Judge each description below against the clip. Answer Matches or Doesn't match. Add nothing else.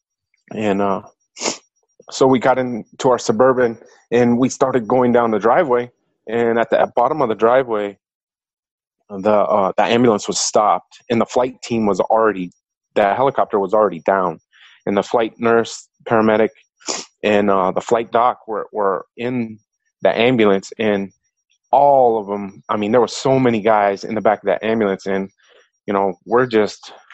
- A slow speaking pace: Doesn't match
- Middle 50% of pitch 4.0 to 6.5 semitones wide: Doesn't match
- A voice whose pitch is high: Doesn't match